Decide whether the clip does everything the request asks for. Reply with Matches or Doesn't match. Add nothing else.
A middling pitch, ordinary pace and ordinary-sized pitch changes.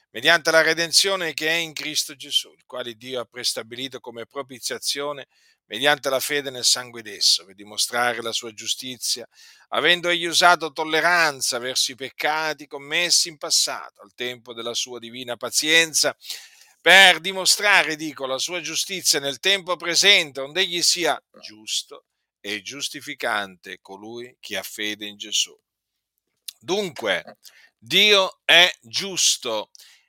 Doesn't match